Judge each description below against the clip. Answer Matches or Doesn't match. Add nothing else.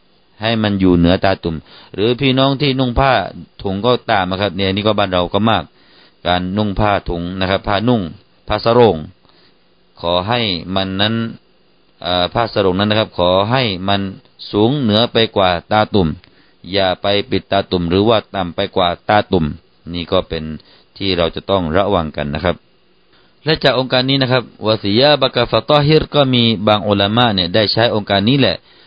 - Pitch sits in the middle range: Doesn't match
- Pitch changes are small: Doesn't match